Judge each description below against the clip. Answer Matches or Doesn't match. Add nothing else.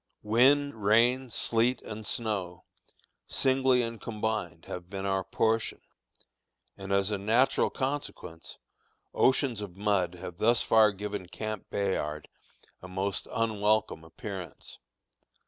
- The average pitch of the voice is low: Matches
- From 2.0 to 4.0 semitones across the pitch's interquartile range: Matches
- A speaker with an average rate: Doesn't match